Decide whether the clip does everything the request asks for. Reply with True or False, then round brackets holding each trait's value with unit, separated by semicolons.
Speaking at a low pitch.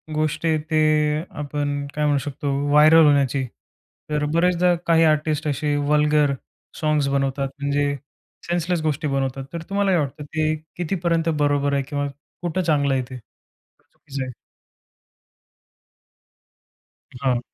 False (150 Hz)